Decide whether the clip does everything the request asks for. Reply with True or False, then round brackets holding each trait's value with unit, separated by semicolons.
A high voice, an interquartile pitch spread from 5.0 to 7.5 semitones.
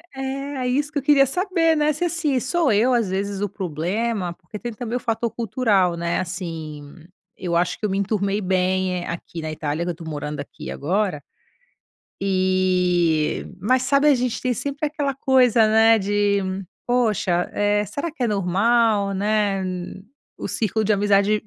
True (205 Hz; 5.4 semitones)